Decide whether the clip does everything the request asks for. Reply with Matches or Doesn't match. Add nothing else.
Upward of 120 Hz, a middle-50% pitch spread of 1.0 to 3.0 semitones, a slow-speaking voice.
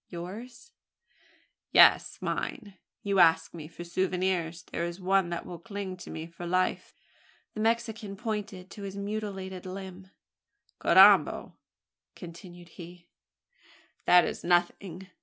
Matches